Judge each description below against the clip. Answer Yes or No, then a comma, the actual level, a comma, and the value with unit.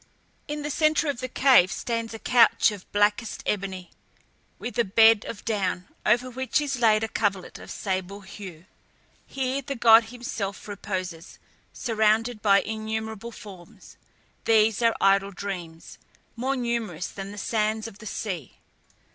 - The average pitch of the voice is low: No, high, 220 Hz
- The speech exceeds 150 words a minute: No, average, 145 wpm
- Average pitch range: Yes, average, 3.3 semitones